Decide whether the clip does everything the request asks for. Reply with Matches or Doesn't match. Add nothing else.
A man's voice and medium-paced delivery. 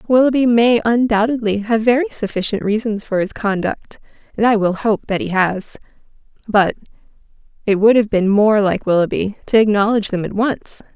Doesn't match